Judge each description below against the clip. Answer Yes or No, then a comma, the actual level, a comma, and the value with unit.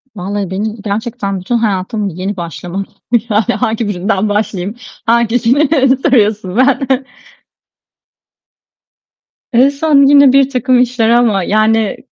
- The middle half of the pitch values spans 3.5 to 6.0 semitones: Yes, average, 4.1 semitones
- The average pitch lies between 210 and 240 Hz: Yes, high, 225 Hz